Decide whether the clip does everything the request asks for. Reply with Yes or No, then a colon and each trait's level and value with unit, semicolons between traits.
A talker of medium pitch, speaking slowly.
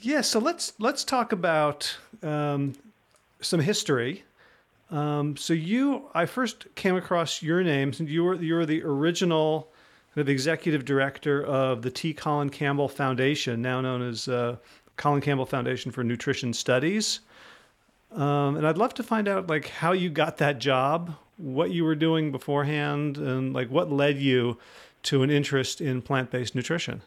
No: medium, 145 Hz; average, 165 wpm